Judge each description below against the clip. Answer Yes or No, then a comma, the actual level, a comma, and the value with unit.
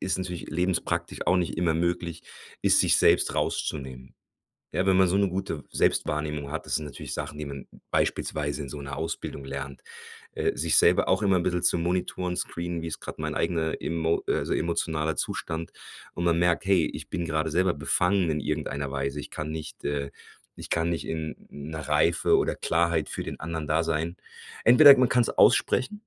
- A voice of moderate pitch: No, very low, 80 Hz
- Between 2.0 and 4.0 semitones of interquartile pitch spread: Yes, average, 2.7 semitones